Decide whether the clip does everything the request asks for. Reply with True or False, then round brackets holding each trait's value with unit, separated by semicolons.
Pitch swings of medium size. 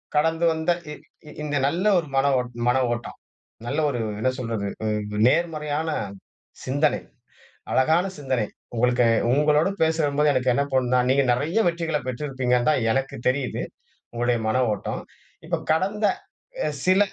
True (4.2 semitones)